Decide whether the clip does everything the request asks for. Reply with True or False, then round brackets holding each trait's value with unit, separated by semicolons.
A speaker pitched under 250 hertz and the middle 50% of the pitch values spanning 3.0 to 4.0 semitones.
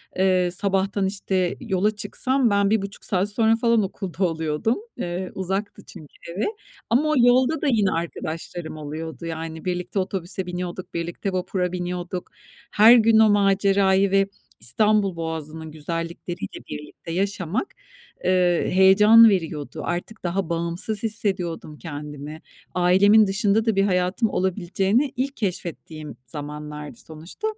True (185 Hz; 3.5 semitones)